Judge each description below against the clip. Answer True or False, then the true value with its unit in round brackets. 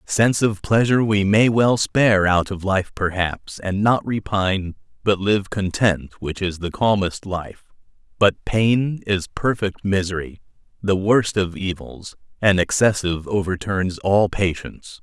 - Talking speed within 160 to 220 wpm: False (145 wpm)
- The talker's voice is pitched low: True (100 Hz)